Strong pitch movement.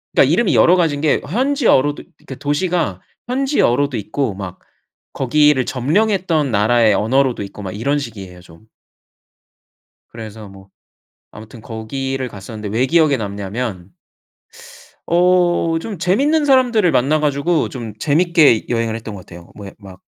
Yes: wide, 7.8 semitones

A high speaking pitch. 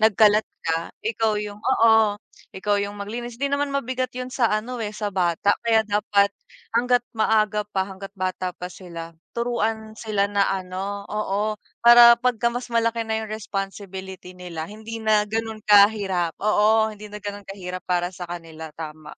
Yes: high, 210 Hz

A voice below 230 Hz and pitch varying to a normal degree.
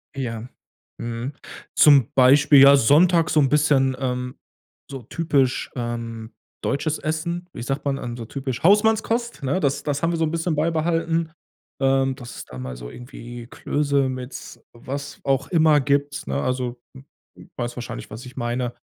Yes: low, 135 Hz; average, 3.7 semitones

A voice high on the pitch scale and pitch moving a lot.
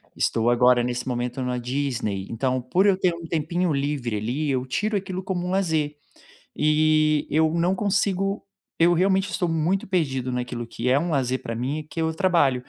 No: medium, 150 Hz; wide, 5.9 semitones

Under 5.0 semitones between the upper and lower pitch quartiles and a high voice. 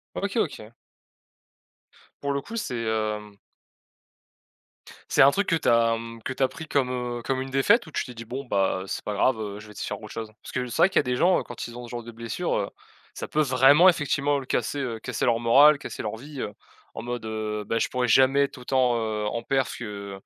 No: average, 3.9 semitones; low, 120 Hz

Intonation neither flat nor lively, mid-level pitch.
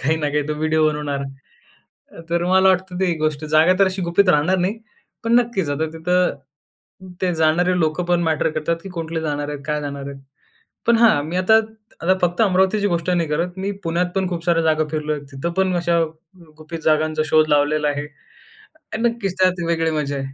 Yes: average, 3.1 semitones; medium, 165 Hz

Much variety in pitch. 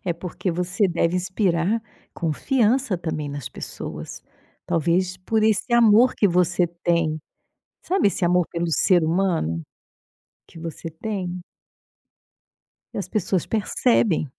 No: average, 3.7 semitones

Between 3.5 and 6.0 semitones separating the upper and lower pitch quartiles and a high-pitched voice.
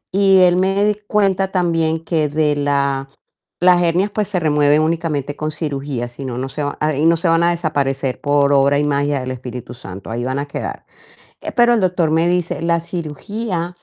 No: average, 3.9 semitones; medium, 155 Hz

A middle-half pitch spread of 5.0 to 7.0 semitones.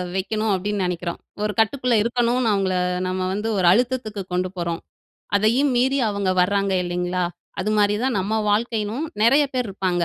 No: average, 4.1 semitones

